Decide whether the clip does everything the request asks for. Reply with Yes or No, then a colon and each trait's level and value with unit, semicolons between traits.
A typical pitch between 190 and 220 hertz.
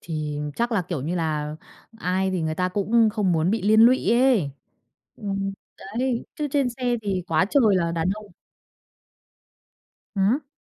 Yes: high, 195 Hz